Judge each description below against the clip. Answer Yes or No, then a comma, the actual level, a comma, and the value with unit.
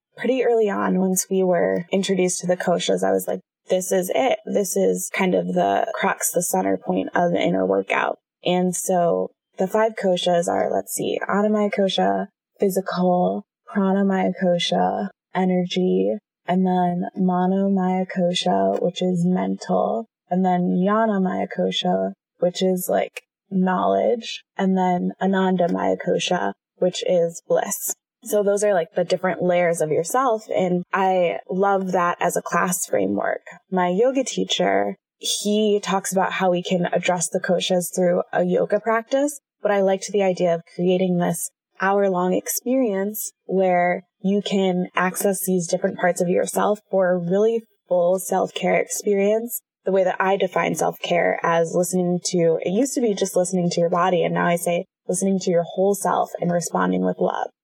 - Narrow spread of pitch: Yes, narrow, 2.0 semitones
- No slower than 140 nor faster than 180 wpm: Yes, average, 165 wpm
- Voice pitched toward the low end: No, medium, 185 Hz